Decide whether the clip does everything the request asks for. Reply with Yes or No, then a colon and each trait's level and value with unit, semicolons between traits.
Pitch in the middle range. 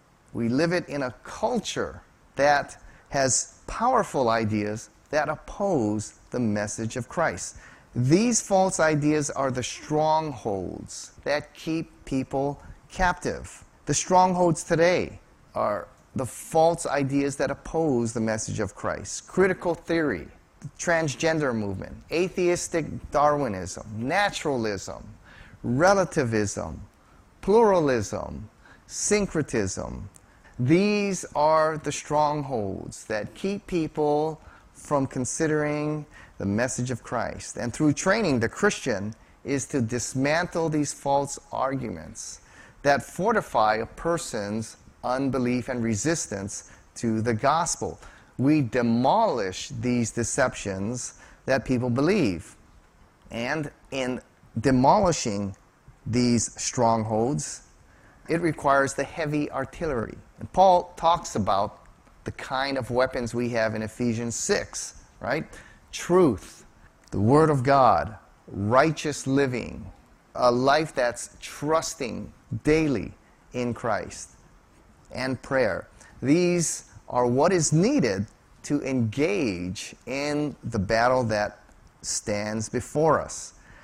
No: low, 130 Hz